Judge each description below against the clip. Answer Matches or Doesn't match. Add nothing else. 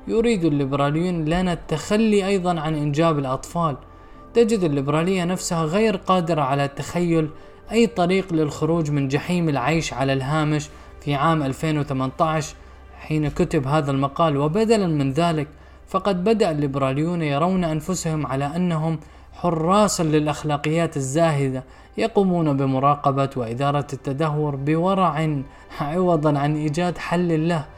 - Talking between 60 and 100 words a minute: Doesn't match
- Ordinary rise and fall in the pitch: Matches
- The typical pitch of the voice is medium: Matches